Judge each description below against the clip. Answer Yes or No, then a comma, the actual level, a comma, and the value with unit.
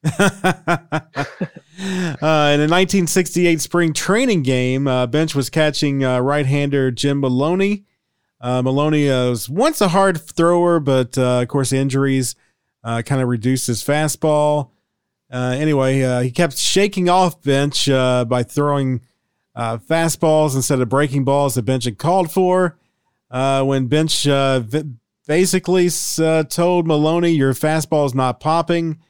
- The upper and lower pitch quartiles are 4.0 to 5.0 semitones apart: Yes, average, 4.5 semitones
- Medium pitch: Yes, medium, 145 Hz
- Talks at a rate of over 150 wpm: No, average, 140 wpm